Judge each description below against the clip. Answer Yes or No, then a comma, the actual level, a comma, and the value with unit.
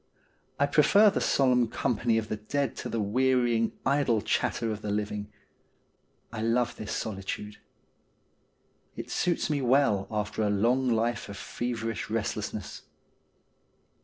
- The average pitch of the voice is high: No, low, 115 Hz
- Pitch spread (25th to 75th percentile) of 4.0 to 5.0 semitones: No, average, 3.4 semitones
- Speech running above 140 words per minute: No, slow, 135 wpm